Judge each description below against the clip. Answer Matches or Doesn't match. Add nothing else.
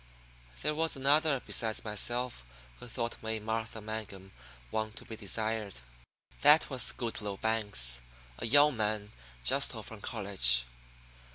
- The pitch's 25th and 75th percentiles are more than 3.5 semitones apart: Doesn't match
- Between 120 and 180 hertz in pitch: Doesn't match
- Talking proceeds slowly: Matches